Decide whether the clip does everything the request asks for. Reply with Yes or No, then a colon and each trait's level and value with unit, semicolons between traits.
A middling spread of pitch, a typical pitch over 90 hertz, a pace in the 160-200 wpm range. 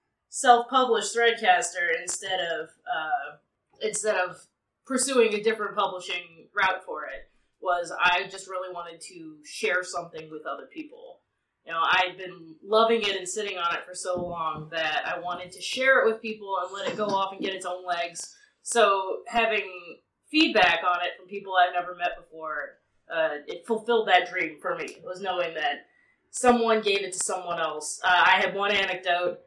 Yes: average, 4.4 semitones; high, 190 Hz; average, 185 wpm